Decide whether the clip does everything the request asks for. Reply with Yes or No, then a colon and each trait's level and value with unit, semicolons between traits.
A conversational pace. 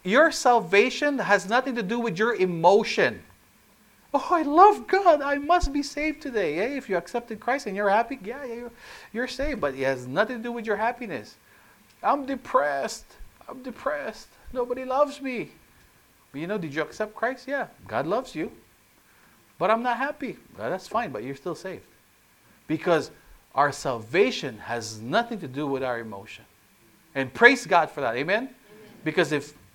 Yes: average, 175 wpm